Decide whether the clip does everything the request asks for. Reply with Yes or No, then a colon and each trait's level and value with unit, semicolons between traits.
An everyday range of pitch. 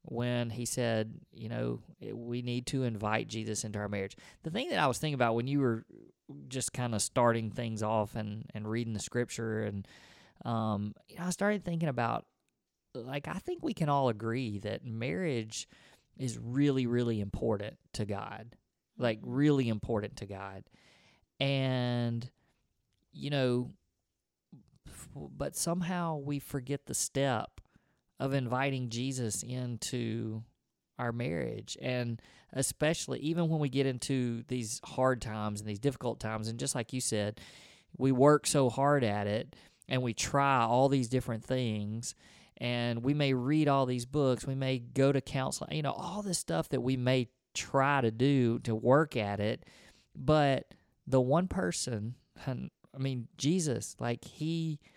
Yes: average, 3.3 semitones